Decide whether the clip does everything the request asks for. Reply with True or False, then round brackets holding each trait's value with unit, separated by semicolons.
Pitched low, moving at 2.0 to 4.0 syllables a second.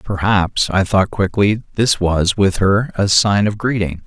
True (100 Hz; 3.8 syllables/s)